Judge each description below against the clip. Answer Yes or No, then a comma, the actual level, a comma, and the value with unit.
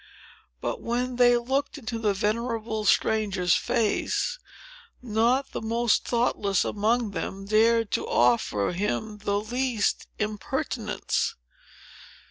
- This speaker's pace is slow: Yes, slow, 105 wpm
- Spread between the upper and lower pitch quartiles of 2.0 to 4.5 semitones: Yes, narrow, 2.6 semitones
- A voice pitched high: Yes, high, 220 Hz